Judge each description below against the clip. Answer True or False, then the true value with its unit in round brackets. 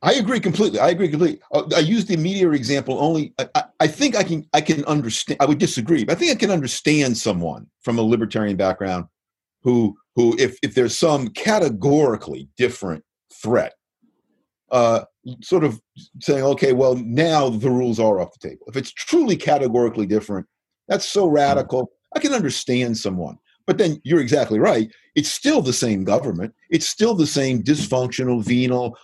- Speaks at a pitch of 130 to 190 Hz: True (135 Hz)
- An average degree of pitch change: False (5.9 semitones)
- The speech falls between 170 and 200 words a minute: True (175 wpm)